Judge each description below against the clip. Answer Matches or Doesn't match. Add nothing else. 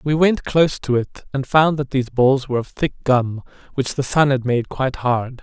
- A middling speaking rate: Doesn't match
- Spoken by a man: Matches